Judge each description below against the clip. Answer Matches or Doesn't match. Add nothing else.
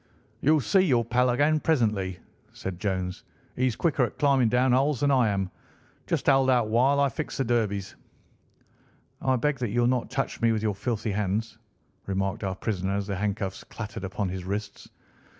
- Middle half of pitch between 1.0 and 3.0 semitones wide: Doesn't match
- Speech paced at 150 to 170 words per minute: Doesn't match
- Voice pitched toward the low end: Matches